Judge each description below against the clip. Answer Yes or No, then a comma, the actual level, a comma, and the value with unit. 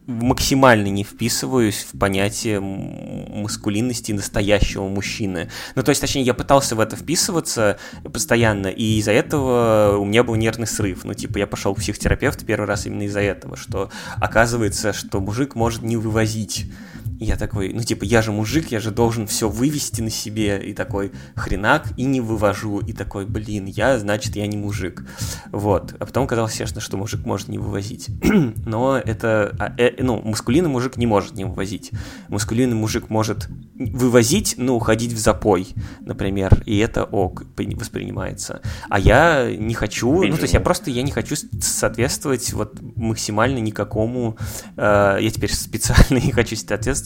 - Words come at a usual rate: No, fast, 165 wpm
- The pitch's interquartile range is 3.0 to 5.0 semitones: No, narrow, 2.6 semitones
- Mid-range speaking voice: No, low, 110 Hz